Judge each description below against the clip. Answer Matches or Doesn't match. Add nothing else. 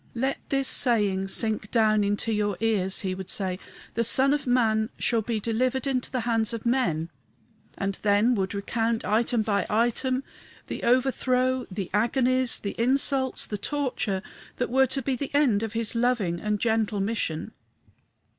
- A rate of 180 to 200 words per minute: Doesn't match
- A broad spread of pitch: Doesn't match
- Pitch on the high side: Matches